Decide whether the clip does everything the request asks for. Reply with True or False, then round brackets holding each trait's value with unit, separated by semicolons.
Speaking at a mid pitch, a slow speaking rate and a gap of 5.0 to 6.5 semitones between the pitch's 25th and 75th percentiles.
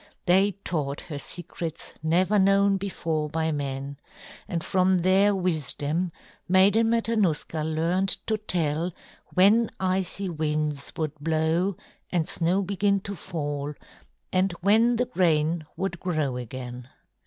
False (175 Hz; 120 wpm; 4.0 semitones)